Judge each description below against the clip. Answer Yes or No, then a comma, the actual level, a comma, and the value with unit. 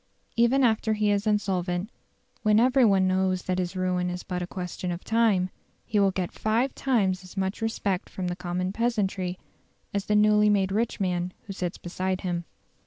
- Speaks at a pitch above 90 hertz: Yes, high, 190 Hz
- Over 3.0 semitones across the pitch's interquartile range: No, average, 2.7 semitones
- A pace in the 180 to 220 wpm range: Yes, average, 185 wpm